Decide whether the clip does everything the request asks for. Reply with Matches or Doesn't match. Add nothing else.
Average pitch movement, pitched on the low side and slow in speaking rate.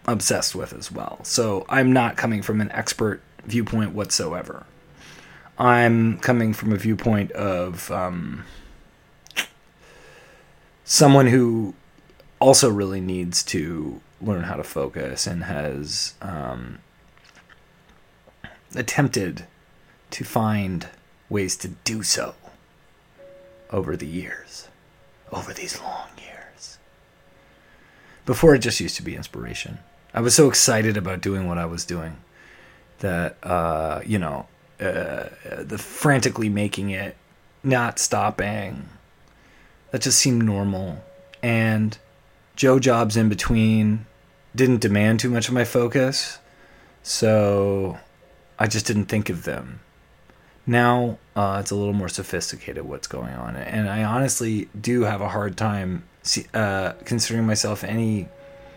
Matches